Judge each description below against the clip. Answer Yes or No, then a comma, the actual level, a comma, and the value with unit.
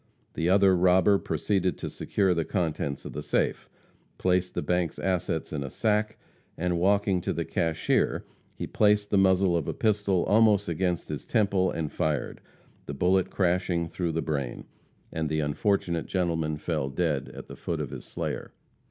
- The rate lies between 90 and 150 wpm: No, average, 170 wpm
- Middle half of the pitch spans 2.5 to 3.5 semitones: Yes, average, 3.2 semitones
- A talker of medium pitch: No, very low, 90 Hz